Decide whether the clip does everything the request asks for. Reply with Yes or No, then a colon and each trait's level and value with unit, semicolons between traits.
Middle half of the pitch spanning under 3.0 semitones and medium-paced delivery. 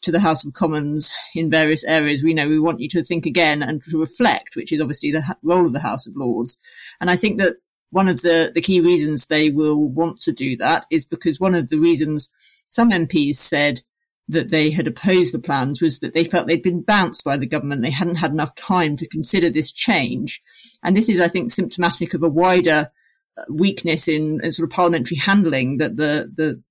No: narrow, 2.6 semitones; fast, 220 wpm